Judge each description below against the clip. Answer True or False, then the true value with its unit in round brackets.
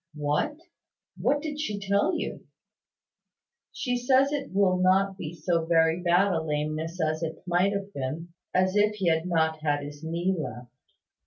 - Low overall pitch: False (175 Hz)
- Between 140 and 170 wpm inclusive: True (165 wpm)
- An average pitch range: True (3.9 semitones)